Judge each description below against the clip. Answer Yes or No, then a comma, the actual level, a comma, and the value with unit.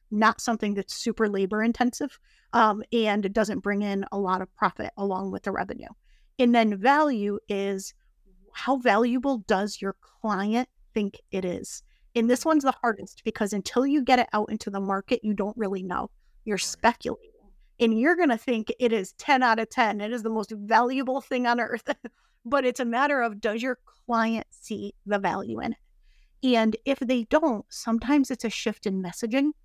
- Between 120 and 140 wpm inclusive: No, average, 190 wpm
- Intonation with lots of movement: No, average, 3.4 semitones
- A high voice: Yes, high, 225 Hz